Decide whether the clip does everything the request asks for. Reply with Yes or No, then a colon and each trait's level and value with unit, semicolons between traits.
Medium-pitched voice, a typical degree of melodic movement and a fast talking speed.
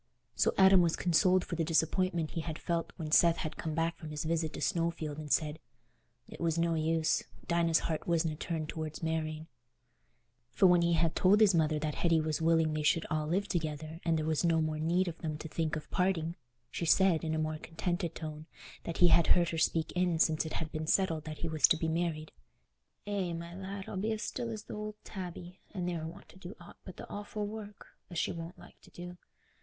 No: medium, 165 Hz; narrow, 2.1 semitones; fast, 225 wpm